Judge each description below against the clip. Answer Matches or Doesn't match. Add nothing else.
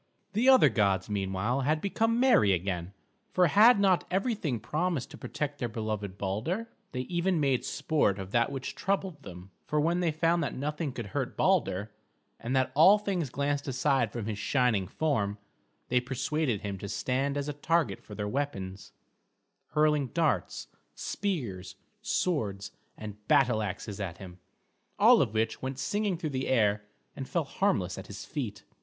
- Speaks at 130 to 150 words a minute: Doesn't match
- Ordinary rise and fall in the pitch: Doesn't match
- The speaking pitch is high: Doesn't match